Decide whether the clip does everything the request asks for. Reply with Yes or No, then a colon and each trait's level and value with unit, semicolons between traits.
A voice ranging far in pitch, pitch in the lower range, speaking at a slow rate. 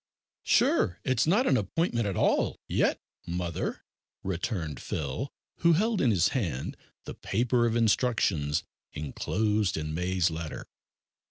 Yes: wide, 6.6 semitones; low, 100 Hz; slow, 125 wpm